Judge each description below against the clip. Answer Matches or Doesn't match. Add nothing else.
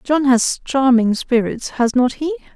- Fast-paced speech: Doesn't match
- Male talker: Doesn't match